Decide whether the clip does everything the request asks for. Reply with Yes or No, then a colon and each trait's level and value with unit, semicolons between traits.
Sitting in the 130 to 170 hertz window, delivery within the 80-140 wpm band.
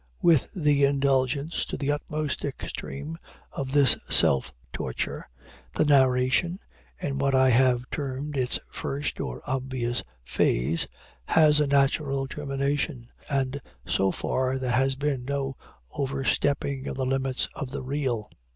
Yes: low, 135 Hz; slow, 135 wpm